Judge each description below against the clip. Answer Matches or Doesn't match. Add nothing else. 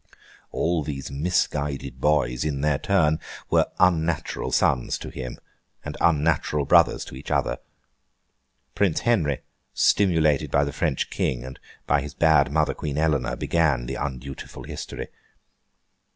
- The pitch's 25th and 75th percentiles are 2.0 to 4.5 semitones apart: Matches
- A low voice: Matches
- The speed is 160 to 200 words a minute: Doesn't match